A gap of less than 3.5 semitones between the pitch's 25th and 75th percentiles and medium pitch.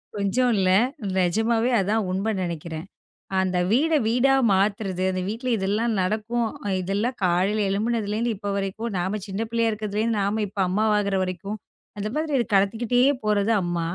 No: average, 3.0 semitones; high, 210 Hz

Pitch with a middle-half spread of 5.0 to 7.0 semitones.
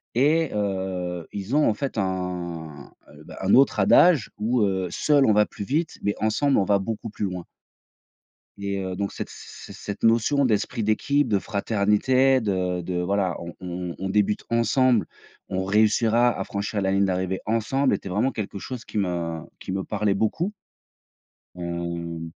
No: average, 3.8 semitones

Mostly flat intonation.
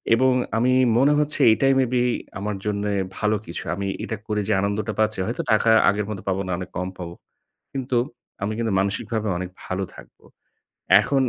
No: average, 3.6 semitones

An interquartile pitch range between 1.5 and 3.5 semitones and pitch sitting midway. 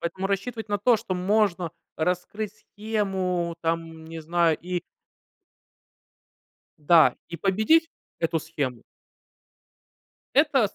No: average, 3.9 semitones; medium, 180 Hz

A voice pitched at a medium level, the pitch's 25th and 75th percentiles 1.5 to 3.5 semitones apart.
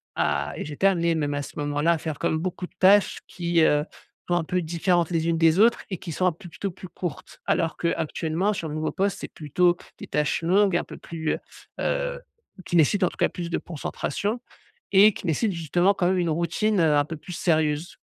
Yes: medium, 170 Hz; average, 2.8 semitones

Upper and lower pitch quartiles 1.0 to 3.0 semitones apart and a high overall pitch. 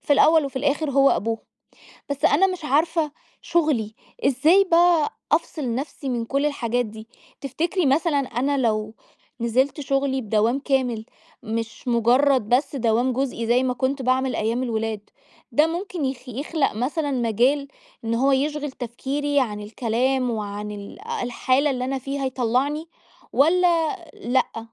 No: average, 3.8 semitones; very high, 265 Hz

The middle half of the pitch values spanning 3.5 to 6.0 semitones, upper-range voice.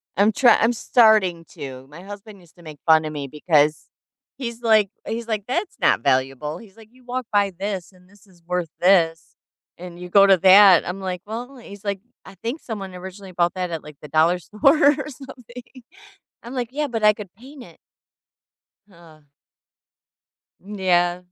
Yes: average, 4.5 semitones; high, 195 Hz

